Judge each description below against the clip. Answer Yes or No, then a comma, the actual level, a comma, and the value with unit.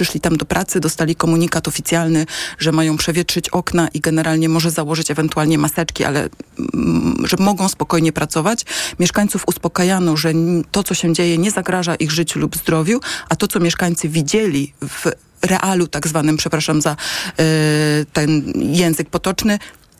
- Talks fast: No, average, 150 wpm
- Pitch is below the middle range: No, medium, 165 Hz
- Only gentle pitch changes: Yes, narrow, 2.2 semitones